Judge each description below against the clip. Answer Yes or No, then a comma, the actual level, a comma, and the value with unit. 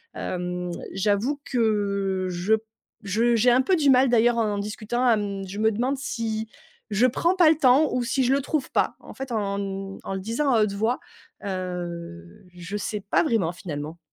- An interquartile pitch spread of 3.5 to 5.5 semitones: Yes, average, 4.3 semitones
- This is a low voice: No, high, 215 Hz